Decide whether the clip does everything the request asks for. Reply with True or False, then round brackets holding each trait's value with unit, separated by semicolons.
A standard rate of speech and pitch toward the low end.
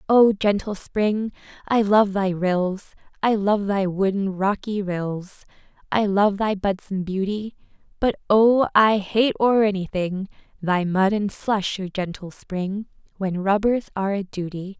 False (145 wpm; 200 Hz)